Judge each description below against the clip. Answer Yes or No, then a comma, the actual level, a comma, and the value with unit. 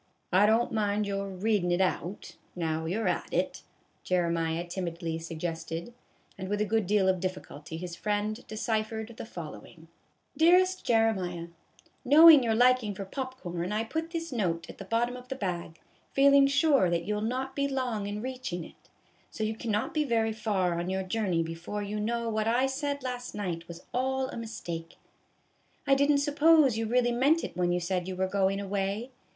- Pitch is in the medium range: No, high, 210 Hz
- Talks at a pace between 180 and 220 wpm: Yes, average, 190 wpm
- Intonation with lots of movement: Yes, wide, 5.8 semitones